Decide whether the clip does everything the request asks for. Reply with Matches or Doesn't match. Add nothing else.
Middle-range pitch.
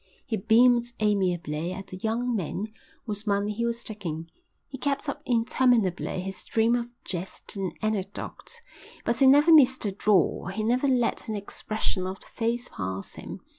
Doesn't match